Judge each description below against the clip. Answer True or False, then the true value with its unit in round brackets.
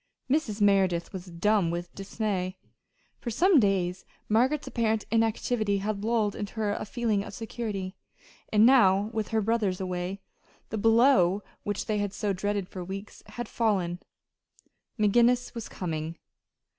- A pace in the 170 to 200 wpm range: False (145 wpm)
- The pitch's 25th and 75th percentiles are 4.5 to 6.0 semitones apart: False (3.0 semitones)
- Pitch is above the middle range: True (205 Hz)